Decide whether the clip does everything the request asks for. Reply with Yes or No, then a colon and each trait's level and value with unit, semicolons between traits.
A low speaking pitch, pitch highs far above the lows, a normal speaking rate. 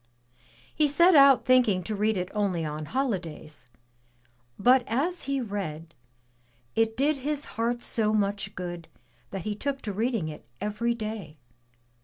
No: high, 215 Hz; wide, 5.7 semitones; average, 145 wpm